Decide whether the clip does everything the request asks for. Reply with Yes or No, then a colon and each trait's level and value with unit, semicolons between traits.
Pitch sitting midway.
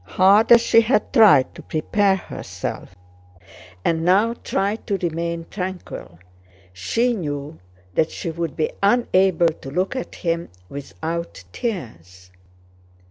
Yes: medium, 175 Hz